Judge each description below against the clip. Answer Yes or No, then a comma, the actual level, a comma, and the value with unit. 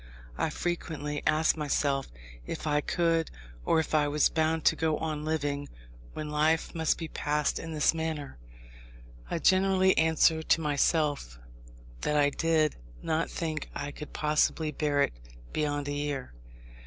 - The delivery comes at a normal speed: Yes, average, 150 wpm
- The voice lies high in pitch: No, medium, 155 Hz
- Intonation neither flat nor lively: No, narrow, 1.7 semitones